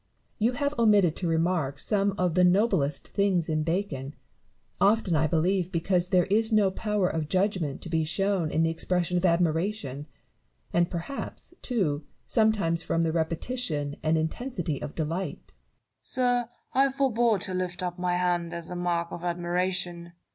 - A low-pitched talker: No, medium, 180 Hz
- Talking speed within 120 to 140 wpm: No, average, 160 wpm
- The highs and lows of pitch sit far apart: No, average, 3.6 semitones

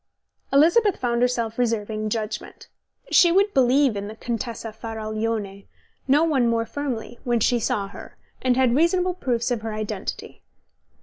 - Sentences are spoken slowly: No, average, 145 wpm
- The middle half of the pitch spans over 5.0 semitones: No, average, 3.6 semitones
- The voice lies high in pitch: Yes, high, 235 Hz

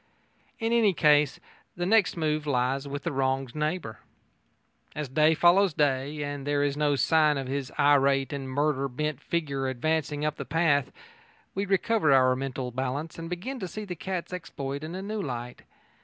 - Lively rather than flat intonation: No, average, 3.5 semitones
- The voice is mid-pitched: Yes, medium, 145 Hz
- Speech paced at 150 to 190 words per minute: Yes, average, 175 wpm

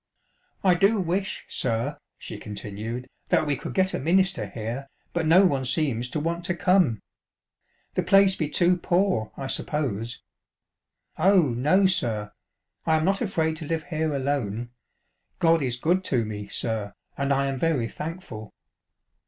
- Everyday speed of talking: Yes, average, 160 wpm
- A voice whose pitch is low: No, medium, 150 Hz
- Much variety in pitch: Yes, wide, 6.7 semitones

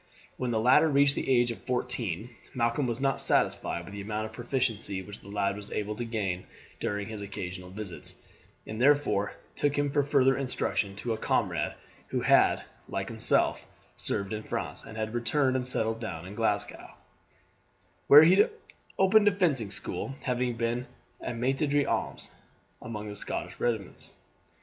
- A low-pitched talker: Yes, low, 115 Hz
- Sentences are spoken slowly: No, average, 165 wpm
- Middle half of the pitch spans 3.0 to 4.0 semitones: No, average, 4.5 semitones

